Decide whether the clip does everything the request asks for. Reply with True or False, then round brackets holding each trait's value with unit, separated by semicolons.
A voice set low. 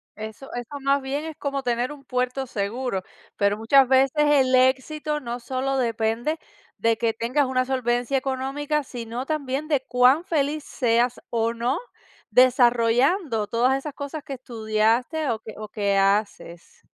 False (255 Hz)